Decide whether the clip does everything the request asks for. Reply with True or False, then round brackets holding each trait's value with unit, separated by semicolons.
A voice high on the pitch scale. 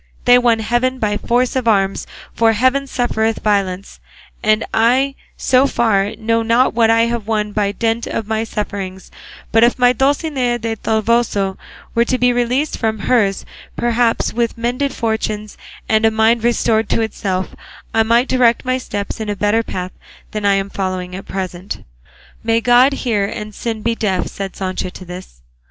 True (225 Hz)